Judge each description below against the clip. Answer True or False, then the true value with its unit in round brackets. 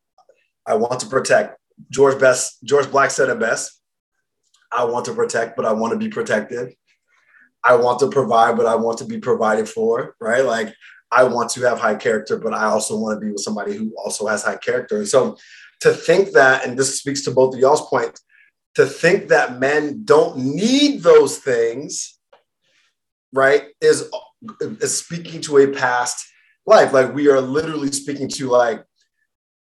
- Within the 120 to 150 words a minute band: False (175 wpm)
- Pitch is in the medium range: True (155 Hz)